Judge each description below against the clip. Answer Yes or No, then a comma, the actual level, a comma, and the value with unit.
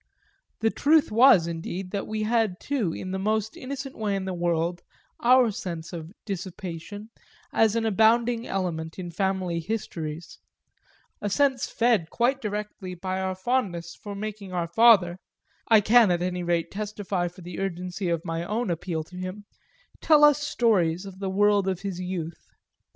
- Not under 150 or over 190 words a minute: Yes, average, 165 wpm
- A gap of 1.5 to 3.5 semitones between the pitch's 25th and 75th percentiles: No, average, 3.9 semitones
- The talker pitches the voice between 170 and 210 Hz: Yes, high, 190 Hz